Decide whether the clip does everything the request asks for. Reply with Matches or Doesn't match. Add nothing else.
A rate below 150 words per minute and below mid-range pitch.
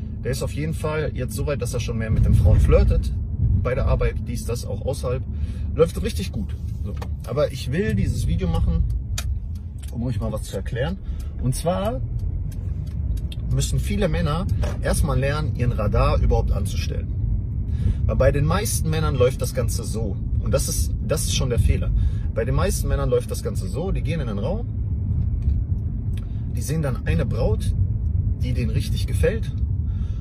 Doesn't match